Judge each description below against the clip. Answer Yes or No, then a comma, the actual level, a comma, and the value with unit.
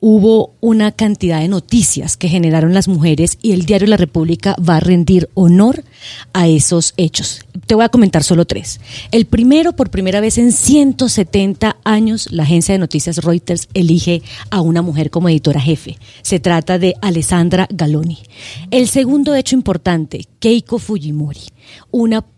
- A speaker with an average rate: Yes, average, 160 wpm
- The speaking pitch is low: No, medium, 180 Hz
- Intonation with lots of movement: No, average, 5.0 semitones